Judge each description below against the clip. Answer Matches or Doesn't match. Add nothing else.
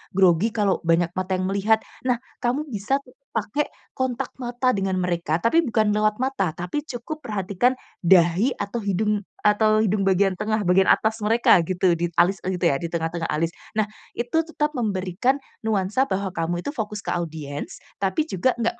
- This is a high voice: Matches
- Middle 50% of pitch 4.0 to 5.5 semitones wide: Matches